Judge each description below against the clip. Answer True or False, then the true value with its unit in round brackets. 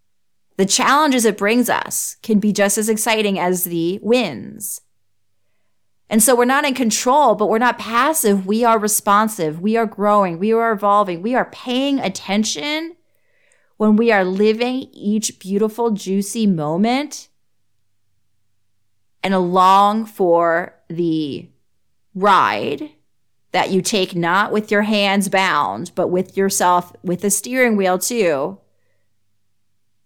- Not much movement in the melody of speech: False (4.9 semitones)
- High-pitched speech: True (200 Hz)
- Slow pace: True (130 wpm)